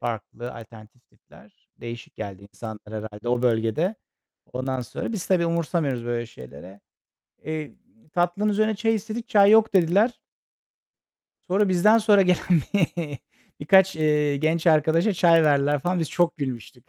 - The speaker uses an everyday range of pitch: No, wide, 7.9 semitones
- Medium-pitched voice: Yes, medium, 160 Hz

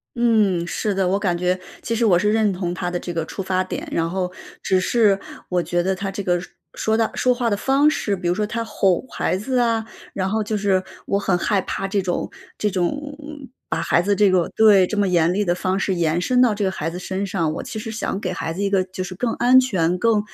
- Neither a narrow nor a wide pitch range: Yes, average, 3.2 semitones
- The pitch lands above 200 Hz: No, high, 195 Hz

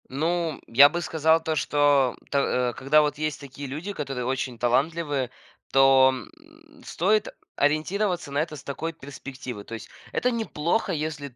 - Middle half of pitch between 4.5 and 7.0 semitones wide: No, average, 3.8 semitones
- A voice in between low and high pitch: Yes, medium, 145 Hz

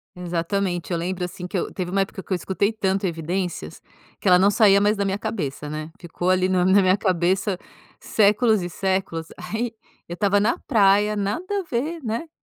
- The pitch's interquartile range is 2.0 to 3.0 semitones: Yes, average, 2.7 semitones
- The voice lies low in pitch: No, high, 195 Hz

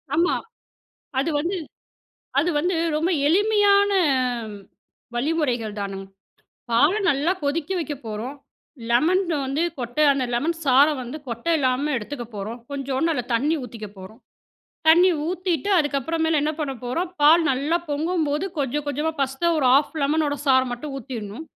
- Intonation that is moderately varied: Yes, average, 4.4 semitones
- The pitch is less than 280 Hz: No, very high, 290 Hz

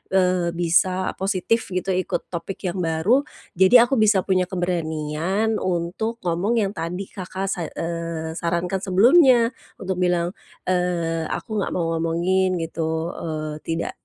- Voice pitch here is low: No, medium, 180 Hz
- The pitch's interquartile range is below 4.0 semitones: Yes, narrow, 2.5 semitones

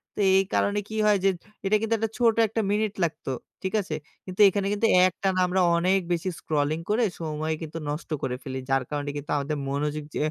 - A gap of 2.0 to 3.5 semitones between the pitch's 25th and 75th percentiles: No, average, 5.2 semitones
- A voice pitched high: No, medium, 175 Hz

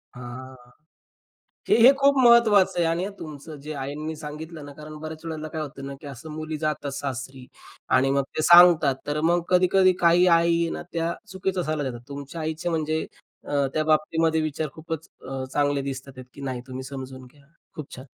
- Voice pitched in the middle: Yes, medium, 155 Hz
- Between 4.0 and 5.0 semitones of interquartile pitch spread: No, average, 3.2 semitones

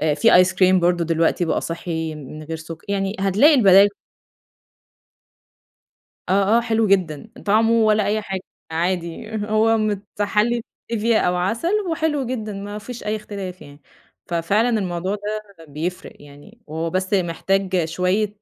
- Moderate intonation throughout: Yes, average, 3.9 semitones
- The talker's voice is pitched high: Yes, high, 195 Hz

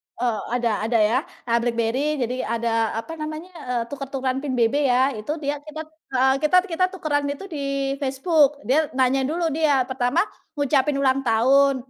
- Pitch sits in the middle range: No, very high, 275 Hz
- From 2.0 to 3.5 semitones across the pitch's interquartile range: Yes, average, 3.2 semitones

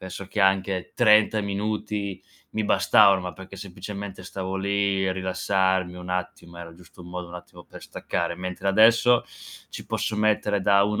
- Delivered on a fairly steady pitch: Yes, narrow, 2.0 semitones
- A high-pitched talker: No, very low, 95 Hz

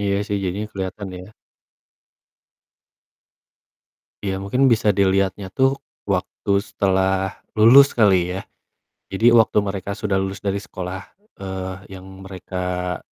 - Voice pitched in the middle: No, very low, 95 Hz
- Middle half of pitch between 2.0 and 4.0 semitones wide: No, narrow, 1.5 semitones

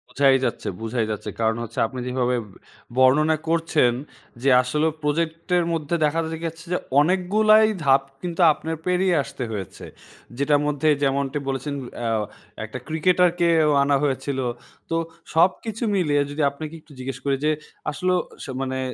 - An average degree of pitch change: Yes, average, 3.9 semitones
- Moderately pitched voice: Yes, medium, 150 Hz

